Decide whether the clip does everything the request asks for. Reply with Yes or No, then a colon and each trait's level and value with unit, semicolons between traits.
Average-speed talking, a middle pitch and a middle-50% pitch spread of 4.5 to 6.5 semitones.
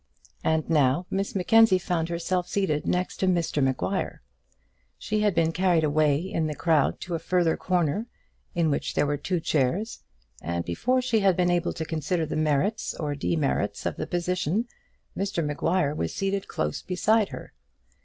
No: average, 170 wpm; medium, 170 Hz; average, 3.7 semitones